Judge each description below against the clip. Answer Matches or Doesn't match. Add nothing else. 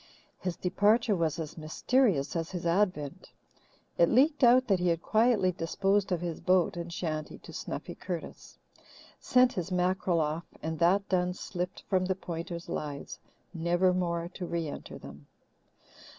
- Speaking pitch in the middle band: Matches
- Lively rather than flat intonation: Doesn't match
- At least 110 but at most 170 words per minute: Matches